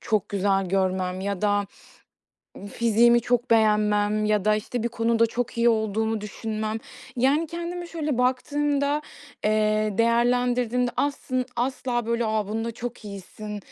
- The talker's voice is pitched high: Yes, high, 230 Hz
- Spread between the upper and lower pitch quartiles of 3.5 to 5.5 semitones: No, average, 2.7 semitones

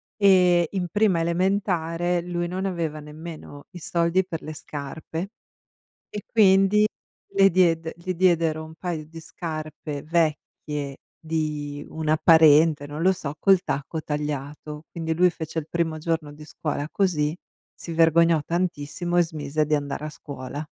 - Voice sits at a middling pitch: Yes, medium, 160 Hz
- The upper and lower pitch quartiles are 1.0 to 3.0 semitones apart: Yes, narrow, 2.6 semitones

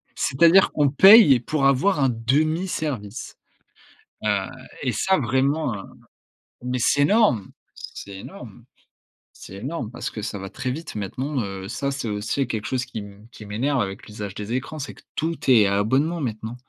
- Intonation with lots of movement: Yes, wide, 5.8 semitones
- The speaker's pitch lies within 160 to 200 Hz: No, low, 125 Hz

